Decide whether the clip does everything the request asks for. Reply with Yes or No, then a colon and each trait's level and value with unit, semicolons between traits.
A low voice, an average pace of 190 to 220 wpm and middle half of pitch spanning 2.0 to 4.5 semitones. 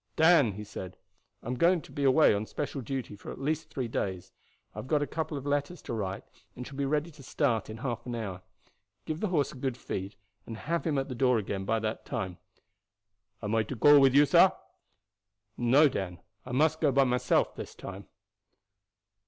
No: low, 130 Hz; fast, 205 wpm; average, 5.1 semitones